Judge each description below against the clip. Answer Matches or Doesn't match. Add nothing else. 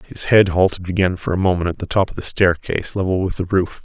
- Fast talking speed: Matches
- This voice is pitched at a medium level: Doesn't match